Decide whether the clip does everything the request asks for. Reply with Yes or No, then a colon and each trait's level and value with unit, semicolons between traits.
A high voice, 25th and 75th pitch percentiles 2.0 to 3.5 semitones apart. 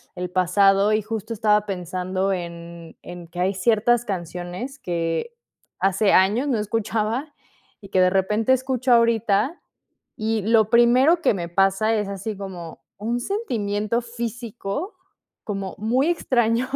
No: high, 210 Hz; average, 3.9 semitones